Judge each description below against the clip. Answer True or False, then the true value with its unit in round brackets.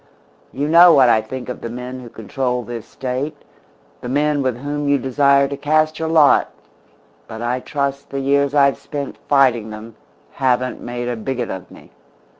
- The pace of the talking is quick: False (180 wpm)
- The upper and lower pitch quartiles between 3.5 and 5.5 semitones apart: False (2.7 semitones)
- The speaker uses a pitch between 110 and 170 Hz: True (135 Hz)